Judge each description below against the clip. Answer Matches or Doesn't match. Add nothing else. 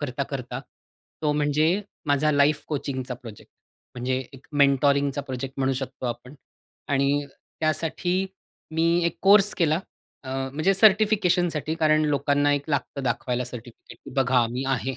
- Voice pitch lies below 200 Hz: Matches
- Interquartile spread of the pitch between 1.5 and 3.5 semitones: Matches